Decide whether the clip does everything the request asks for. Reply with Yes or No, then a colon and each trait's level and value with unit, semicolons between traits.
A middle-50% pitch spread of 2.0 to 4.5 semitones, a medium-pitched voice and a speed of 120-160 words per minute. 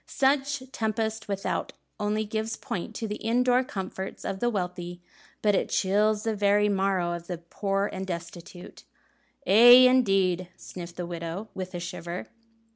No: average, 3.6 semitones; high, 195 Hz; average, 150 wpm